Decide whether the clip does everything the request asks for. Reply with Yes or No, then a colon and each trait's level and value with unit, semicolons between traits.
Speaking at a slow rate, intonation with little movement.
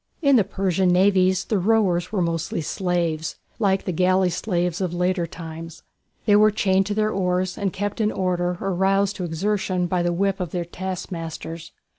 No: average, 180 wpm; narrow, 2.1 semitones